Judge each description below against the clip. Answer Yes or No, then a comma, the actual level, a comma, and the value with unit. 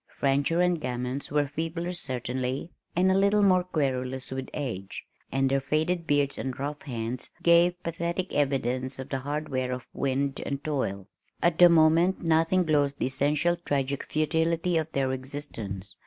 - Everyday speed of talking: Yes, average, 160 wpm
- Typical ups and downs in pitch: Yes, average, 4.1 semitones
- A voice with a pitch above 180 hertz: No, medium, 145 Hz